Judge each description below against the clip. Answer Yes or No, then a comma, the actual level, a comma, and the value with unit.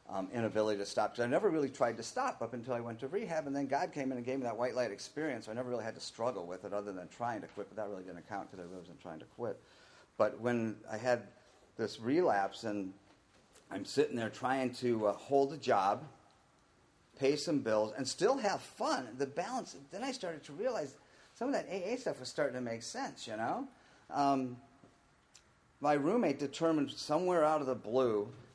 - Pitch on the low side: Yes, low, 125 Hz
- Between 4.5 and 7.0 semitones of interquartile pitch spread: Yes, average, 4.8 semitones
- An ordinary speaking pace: No, fast, 220 wpm